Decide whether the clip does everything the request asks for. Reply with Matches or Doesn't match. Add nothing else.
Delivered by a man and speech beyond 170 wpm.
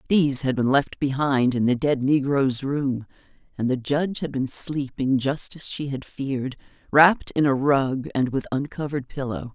Doesn't match